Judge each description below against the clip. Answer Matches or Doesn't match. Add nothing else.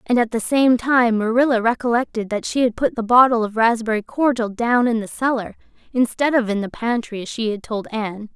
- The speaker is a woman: Matches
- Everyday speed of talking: Doesn't match